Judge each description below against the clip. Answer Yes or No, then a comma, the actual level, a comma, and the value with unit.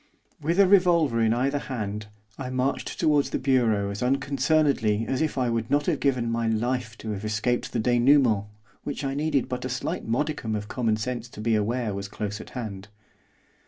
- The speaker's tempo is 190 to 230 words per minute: Yes, average, 195 wpm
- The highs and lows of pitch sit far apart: No, average, 4.1 semitones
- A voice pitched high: No, low, 125 Hz